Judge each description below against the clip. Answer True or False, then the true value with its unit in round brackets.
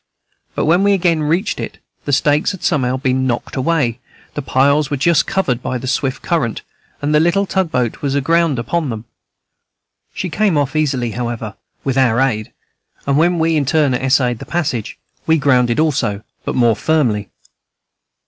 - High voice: False (140 Hz)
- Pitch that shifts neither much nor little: True (4.5 semitones)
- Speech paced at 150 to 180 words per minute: True (175 wpm)